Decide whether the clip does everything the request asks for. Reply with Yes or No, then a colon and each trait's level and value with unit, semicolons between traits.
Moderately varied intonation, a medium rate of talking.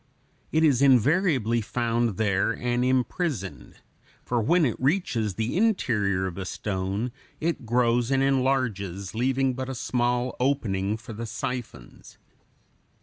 No: average, 3.9 semitones; slow, 130 wpm